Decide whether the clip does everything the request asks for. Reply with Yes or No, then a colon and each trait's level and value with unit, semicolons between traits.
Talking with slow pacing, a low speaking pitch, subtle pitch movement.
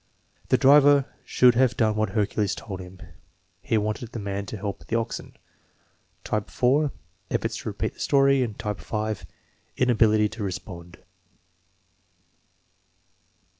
No: slow, 130 wpm; low, 110 Hz; average, 3.6 semitones